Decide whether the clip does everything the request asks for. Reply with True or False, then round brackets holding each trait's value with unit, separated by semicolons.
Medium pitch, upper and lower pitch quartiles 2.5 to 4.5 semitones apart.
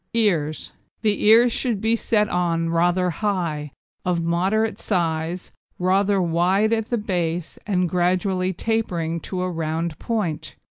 True (180 Hz; 3.8 semitones)